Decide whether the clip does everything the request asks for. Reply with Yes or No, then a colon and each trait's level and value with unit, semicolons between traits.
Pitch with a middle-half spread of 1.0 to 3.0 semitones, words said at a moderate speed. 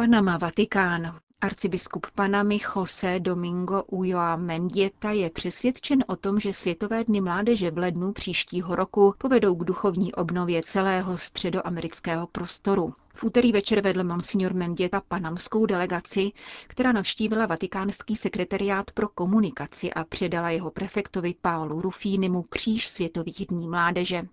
Yes: narrow, 2.6 semitones; average, 125 wpm